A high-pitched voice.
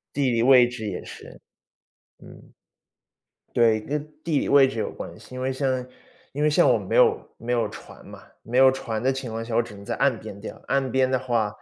No: low, 125 Hz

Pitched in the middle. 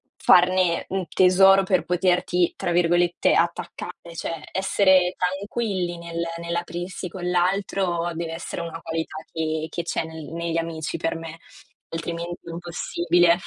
Yes: medium, 175 Hz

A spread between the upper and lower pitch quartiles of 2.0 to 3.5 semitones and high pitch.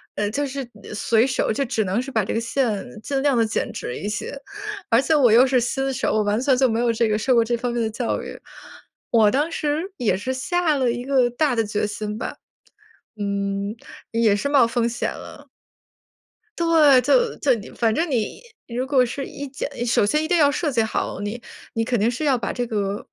No: average, 3.9 semitones; high, 240 Hz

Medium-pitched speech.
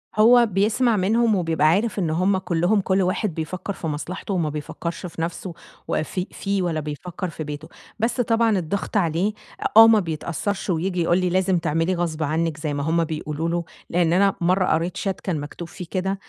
Yes: medium, 180 Hz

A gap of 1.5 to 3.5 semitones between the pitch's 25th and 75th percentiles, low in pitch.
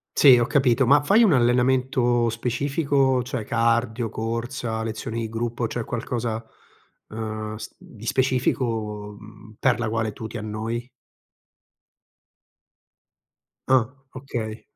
Yes: narrow, 2.4 semitones; low, 115 Hz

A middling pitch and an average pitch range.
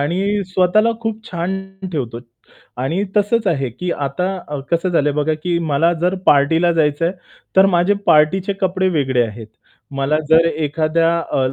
Yes: medium, 165 Hz; average, 4.2 semitones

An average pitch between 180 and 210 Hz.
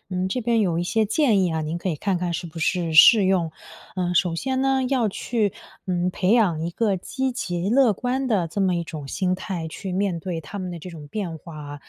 Yes: medium, 185 Hz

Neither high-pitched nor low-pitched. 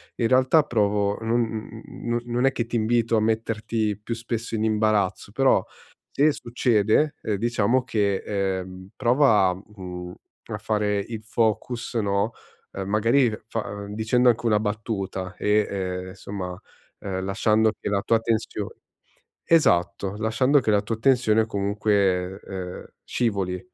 No: low, 110 Hz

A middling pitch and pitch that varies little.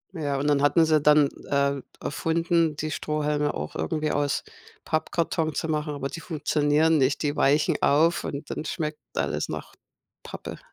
Yes: medium, 150 Hz; narrow, 1.6 semitones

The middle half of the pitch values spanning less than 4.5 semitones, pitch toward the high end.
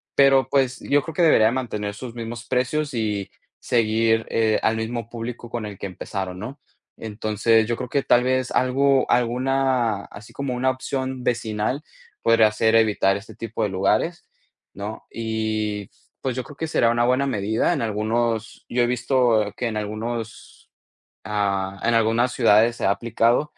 No: average, 2.9 semitones; low, 115 Hz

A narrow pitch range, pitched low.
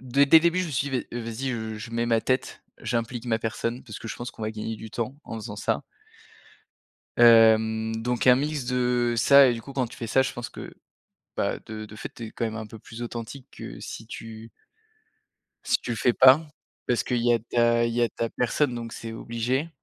Yes: narrow, 1.9 semitones; low, 120 Hz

